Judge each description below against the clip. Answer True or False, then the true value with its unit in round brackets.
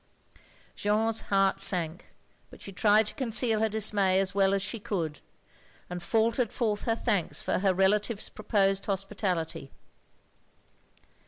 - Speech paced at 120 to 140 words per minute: True (135 wpm)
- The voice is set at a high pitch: True (200 Hz)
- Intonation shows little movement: True (2.3 semitones)